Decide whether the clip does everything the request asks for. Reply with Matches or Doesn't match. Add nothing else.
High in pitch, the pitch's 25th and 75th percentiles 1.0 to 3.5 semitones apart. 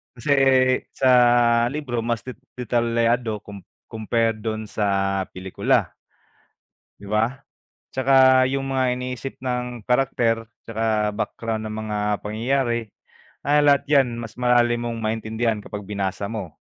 Doesn't match